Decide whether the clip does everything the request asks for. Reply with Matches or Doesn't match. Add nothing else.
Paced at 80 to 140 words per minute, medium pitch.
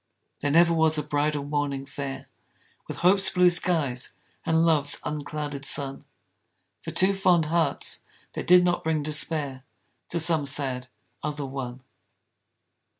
Matches